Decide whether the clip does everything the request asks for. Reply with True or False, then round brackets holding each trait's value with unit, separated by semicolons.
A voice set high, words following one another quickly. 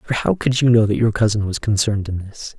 False (110 Hz; 280 wpm)